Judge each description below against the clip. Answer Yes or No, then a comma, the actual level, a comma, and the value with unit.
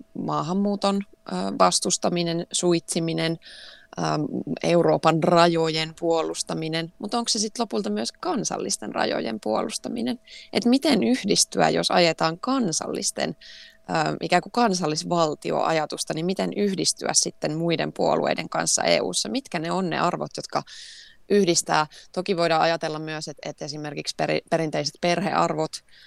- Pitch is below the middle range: No, medium, 175 Hz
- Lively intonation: No, average, 4.5 semitones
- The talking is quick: No, average, 110 wpm